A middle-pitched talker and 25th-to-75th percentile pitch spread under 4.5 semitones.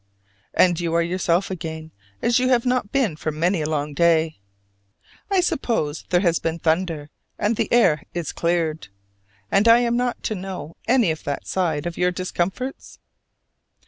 No: medium, 175 Hz; average, 5.3 semitones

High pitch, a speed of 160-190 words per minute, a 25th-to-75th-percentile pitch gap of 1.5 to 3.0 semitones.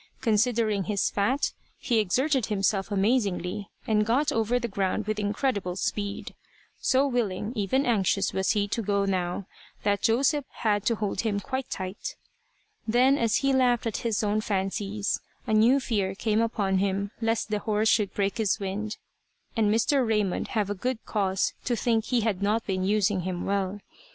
Yes: high, 210 Hz; average, 170 wpm; average, 2.7 semitones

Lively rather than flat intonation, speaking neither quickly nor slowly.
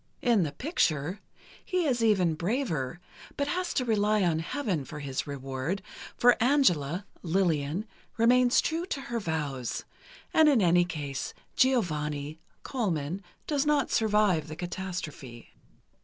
No: wide, 8.2 semitones; slow, 130 wpm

